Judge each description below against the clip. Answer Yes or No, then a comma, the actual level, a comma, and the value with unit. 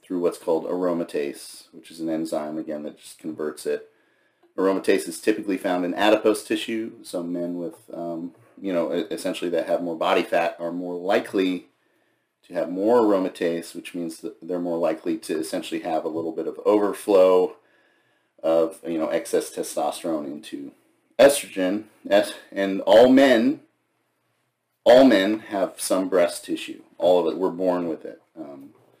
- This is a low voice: Yes, low, 110 Hz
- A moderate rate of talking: Yes, average, 160 wpm